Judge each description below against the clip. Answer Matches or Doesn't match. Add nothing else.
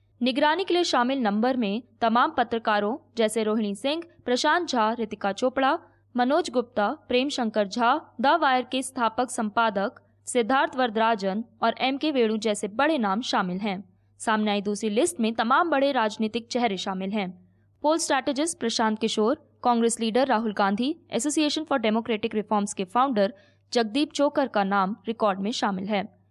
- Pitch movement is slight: Doesn't match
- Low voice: Doesn't match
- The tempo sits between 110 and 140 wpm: Doesn't match